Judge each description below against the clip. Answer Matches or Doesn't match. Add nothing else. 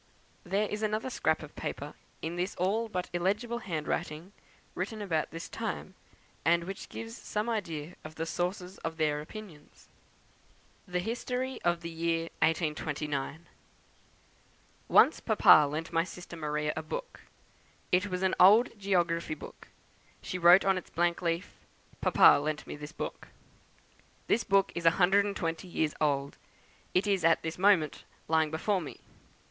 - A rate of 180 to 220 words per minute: Doesn't match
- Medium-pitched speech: Matches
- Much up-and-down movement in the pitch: Doesn't match